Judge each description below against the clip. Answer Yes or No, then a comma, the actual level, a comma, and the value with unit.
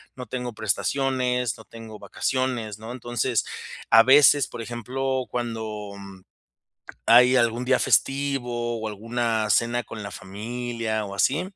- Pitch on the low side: Yes, low, 120 Hz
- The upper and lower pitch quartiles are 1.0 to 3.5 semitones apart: Yes, narrow, 2.4 semitones